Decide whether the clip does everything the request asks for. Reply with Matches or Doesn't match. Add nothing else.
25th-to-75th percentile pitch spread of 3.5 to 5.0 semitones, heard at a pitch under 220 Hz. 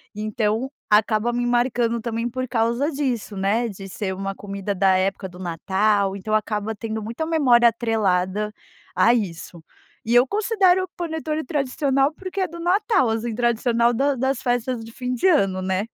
Doesn't match